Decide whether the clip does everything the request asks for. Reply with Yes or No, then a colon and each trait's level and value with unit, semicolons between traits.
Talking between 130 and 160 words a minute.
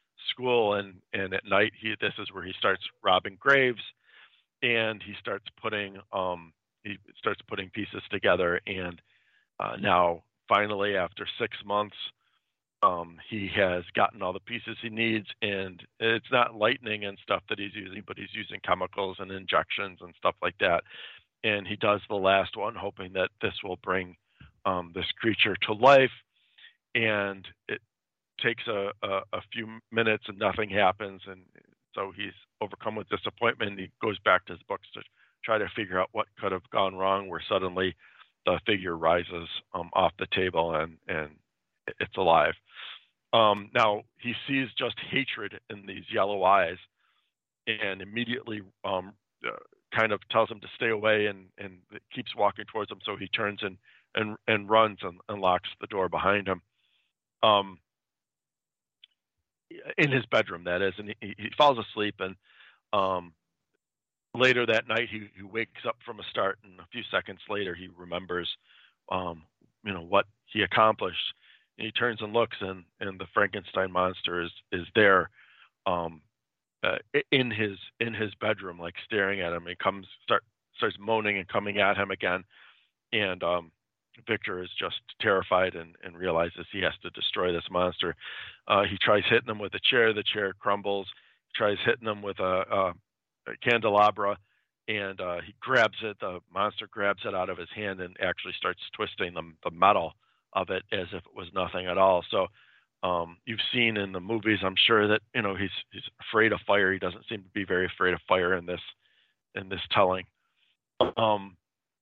No: average, 175 wpm